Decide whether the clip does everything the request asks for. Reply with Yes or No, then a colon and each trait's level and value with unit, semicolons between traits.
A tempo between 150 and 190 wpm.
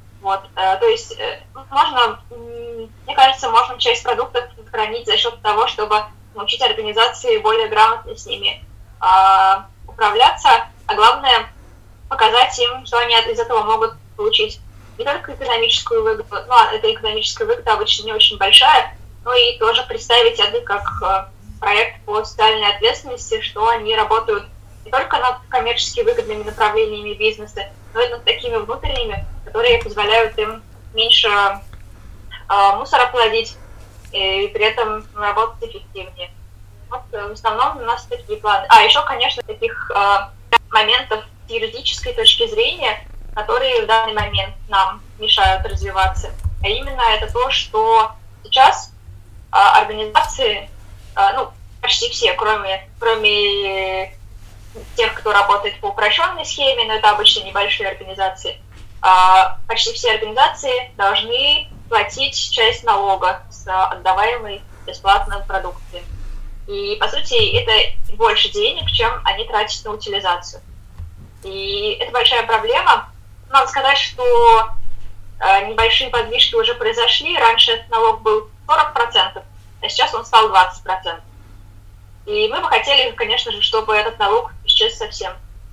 No: average, 130 wpm